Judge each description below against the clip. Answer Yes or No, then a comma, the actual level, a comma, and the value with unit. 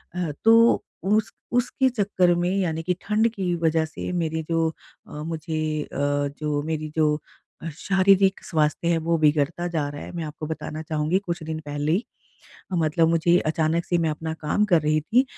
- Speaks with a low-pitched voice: No, medium, 165 Hz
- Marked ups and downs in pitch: No, average, 2.7 semitones